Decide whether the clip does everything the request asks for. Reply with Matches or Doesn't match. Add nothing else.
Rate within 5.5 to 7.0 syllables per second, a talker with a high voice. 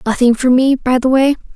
Matches